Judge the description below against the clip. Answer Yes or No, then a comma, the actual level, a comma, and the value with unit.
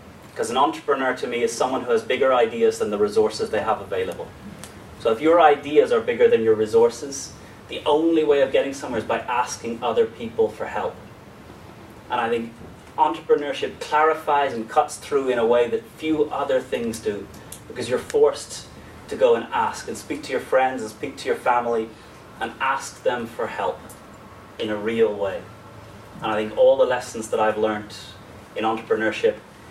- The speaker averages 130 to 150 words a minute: No, average, 185 wpm